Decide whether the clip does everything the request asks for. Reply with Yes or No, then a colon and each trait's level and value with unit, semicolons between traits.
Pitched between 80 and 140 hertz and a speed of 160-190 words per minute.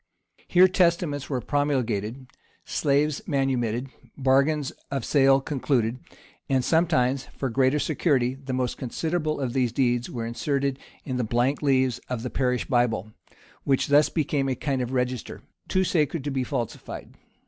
No: low, 135 Hz; average, 150 wpm